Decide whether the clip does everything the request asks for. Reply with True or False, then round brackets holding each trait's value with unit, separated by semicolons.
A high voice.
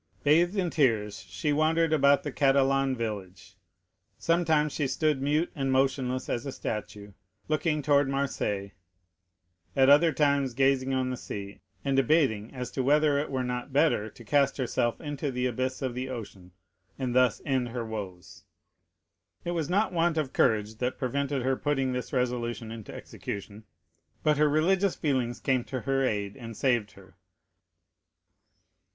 False (130 Hz)